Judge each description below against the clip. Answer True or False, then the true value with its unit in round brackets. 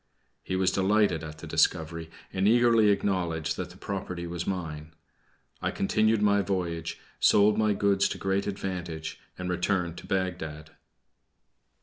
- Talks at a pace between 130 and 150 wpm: True (140 wpm)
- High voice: False (95 Hz)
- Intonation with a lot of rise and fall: False (3.3 semitones)